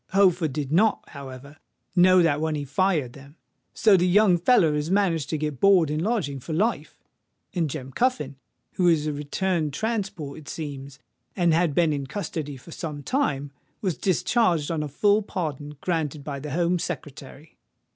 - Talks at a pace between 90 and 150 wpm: No, average, 175 wpm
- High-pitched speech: No, medium, 160 Hz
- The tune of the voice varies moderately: Yes, average, 4.2 semitones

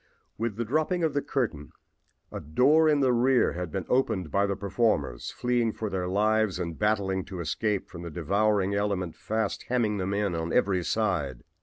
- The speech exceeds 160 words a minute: Yes, average, 185 wpm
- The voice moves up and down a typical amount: Yes, average, 4.4 semitones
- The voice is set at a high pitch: No, low, 100 Hz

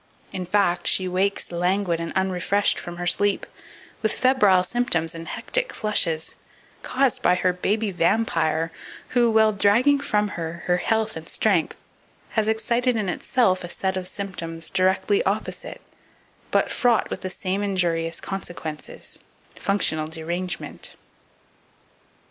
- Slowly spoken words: Yes, slow, 130 wpm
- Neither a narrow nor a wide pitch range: Yes, average, 3.9 semitones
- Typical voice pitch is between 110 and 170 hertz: No, high, 190 Hz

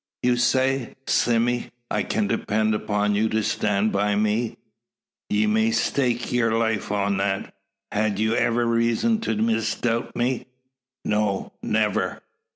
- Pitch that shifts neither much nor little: No, narrow, 2.3 semitones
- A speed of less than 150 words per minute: Yes, slow, 135 wpm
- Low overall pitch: Yes, low, 110 Hz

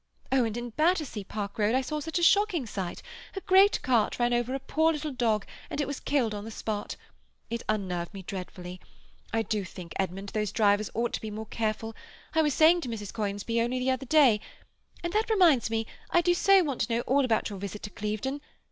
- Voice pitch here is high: Yes, high, 235 Hz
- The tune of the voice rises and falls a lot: Yes, wide, 5.8 semitones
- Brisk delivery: Yes, fast, 220 wpm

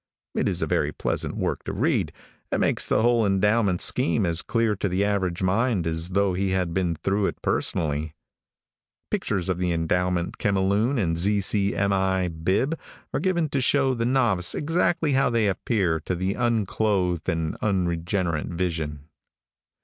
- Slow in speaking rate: No, average, 165 wpm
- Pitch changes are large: No, average, 4.0 semitones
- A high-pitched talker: No, very low, 95 Hz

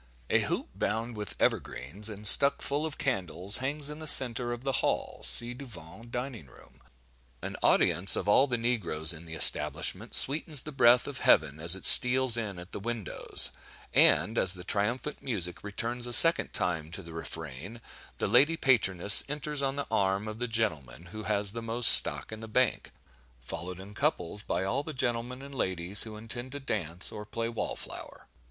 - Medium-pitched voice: No, low, 115 Hz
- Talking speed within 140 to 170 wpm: No, average, 185 wpm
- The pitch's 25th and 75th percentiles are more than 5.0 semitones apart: Yes, wide, 5.4 semitones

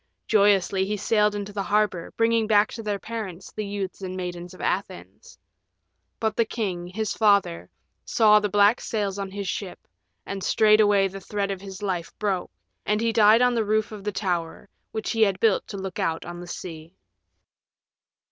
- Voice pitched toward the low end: No, high, 205 Hz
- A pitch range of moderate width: No, narrow, 2.2 semitones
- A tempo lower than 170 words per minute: No, average, 185 wpm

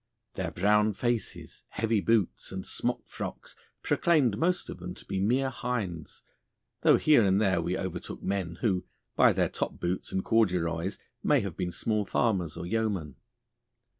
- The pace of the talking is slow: No, average, 155 wpm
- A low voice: Yes, low, 100 Hz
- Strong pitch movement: No, average, 4.0 semitones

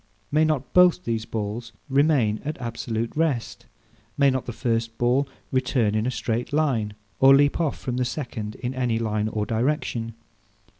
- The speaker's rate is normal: Yes, average, 165 wpm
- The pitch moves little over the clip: No, average, 3.8 semitones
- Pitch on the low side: Yes, low, 125 Hz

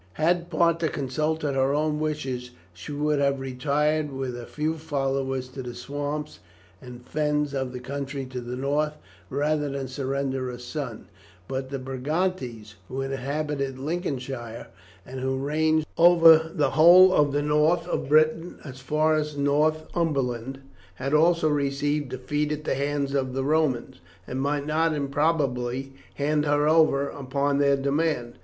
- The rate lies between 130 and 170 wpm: Yes, average, 150 wpm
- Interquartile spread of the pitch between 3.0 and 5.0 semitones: No, narrow, 2.5 semitones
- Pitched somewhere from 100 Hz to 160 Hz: Yes, medium, 140 Hz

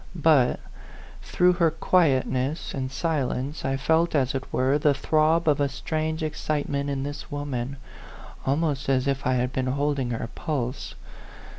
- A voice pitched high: No, medium, 140 Hz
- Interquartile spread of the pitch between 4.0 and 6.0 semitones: No, average, 2.8 semitones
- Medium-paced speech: Yes, average, 155 wpm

